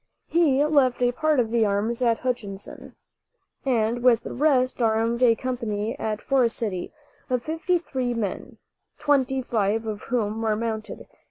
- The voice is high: Yes, high, 235 Hz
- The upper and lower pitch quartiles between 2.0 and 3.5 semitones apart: Yes, average, 2.8 semitones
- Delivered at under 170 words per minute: Yes, average, 155 wpm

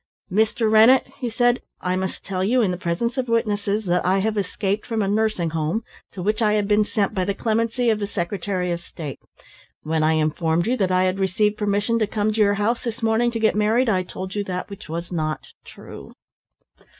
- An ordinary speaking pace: No, fast, 220 wpm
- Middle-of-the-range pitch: No, high, 205 Hz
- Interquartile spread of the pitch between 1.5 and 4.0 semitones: Yes, average, 3.3 semitones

